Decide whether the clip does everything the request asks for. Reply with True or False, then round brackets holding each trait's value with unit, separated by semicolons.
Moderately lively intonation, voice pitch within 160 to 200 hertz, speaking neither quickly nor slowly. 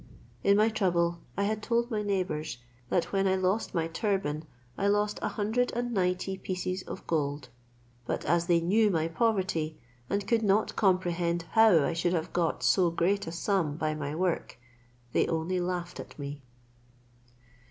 True (3.4 semitones; 185 Hz; 170 wpm)